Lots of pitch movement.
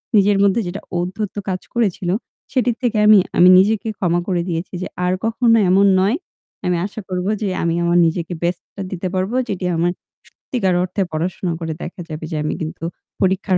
No: average, 2.7 semitones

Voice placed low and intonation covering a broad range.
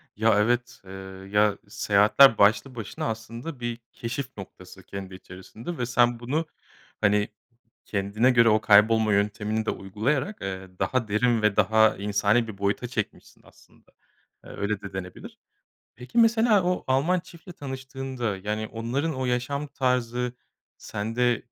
No: low, 115 Hz; average, 3.8 semitones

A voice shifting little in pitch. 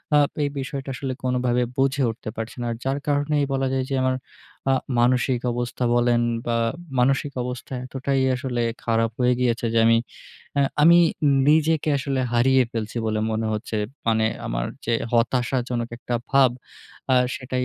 Yes: narrow, 2.3 semitones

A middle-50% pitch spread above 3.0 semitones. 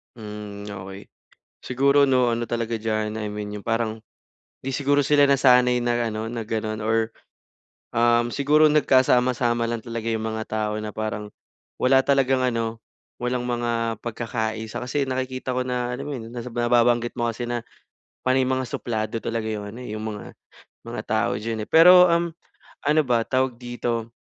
No: narrow, 2.5 semitones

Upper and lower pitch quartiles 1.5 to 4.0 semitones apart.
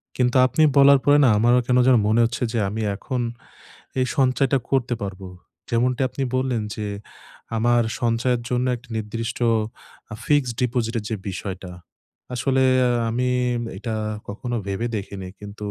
Yes: average, 2.9 semitones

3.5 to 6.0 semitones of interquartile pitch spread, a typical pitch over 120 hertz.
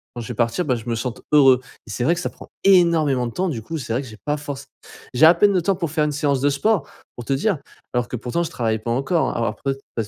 Yes: wide, 5.4 semitones; medium, 140 Hz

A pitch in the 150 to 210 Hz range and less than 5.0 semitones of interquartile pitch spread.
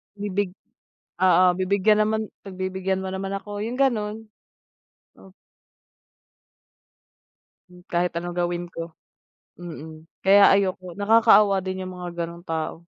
Yes: high, 190 Hz; narrow, 2.5 semitones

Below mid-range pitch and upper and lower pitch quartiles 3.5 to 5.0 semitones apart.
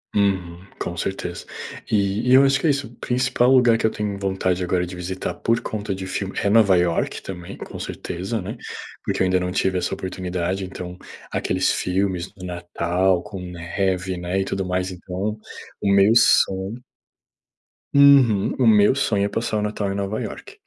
No: very low, 95 Hz; average, 2.8 semitones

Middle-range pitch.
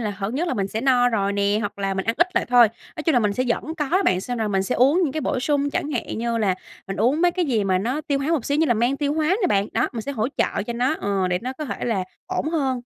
No: high, 245 Hz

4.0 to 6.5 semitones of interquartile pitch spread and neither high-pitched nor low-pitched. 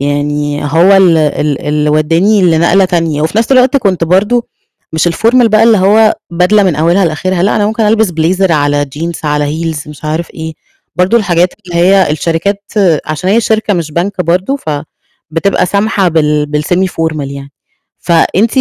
Yes: average, 4.4 semitones; medium, 175 Hz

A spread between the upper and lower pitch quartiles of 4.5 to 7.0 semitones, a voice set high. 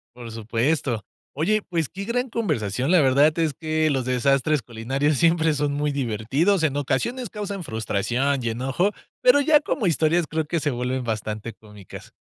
No: wide, 5.5 semitones; medium, 145 Hz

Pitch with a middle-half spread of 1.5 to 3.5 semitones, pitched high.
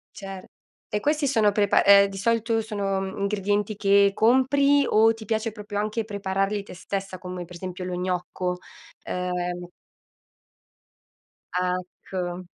Yes: average, 2.9 semitones; high, 200 Hz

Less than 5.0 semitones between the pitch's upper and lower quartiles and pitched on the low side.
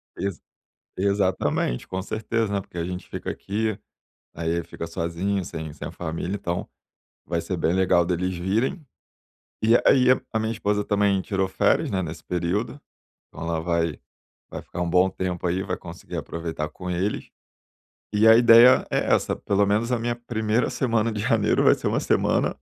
Yes: average, 4.0 semitones; very low, 95 Hz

